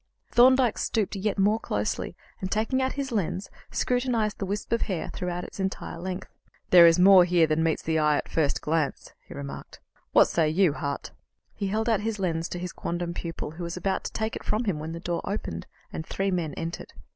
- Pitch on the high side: No, medium, 180 Hz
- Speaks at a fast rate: Yes, fast, 215 wpm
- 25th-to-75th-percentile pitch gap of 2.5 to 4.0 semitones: No, average, 4.4 semitones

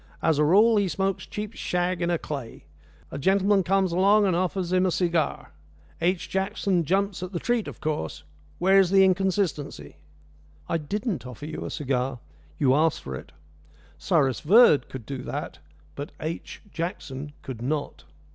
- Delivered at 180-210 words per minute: No, average, 165 wpm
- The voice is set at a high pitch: No, medium, 175 Hz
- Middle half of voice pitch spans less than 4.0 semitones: No, average, 4.8 semitones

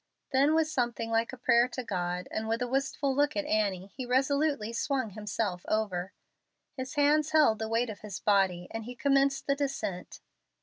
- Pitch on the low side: No, high, 240 Hz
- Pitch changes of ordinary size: Yes, average, 4.8 semitones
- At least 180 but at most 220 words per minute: Yes, average, 185 wpm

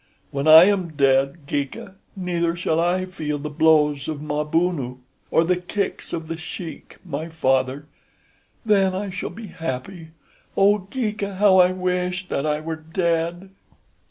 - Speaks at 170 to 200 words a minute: No, average, 150 wpm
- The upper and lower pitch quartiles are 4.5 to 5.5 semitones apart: No, average, 3.5 semitones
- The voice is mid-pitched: Yes, medium, 165 Hz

